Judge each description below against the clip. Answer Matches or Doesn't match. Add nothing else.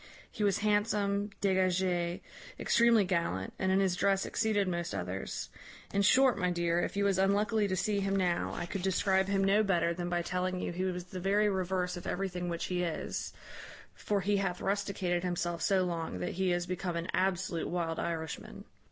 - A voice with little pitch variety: Matches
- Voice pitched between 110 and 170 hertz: Doesn't match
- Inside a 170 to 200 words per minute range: Matches